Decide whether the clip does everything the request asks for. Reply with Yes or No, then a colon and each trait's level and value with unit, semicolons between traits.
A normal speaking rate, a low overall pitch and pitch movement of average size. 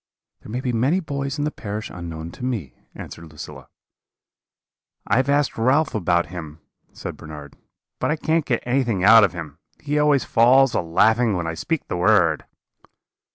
No: average, 175 wpm; low, 115 Hz; wide, 8.1 semitones